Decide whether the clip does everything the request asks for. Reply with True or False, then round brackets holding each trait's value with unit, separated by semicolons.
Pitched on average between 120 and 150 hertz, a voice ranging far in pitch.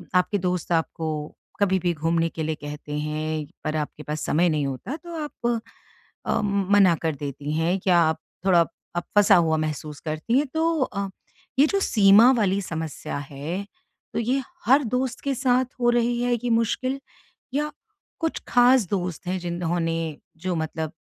False (180 Hz; 7.1 semitones)